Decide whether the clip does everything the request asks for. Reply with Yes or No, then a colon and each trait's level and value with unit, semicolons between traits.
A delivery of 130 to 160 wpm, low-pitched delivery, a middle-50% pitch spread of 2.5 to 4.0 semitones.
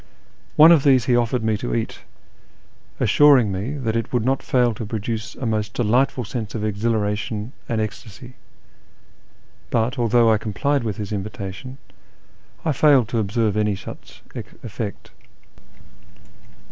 Yes: average, 140 wpm; low, 115 Hz; average, 3.1 semitones